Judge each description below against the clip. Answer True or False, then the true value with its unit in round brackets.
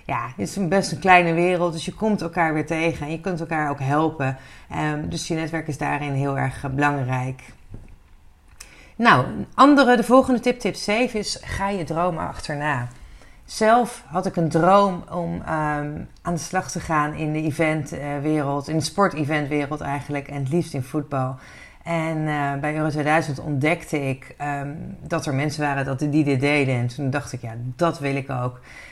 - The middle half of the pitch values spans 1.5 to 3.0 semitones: False (3.4 semitones)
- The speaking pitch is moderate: True (150 Hz)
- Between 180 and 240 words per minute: True (185 wpm)